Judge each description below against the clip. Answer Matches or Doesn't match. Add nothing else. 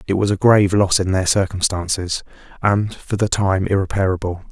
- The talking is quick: Doesn't match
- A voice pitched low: Matches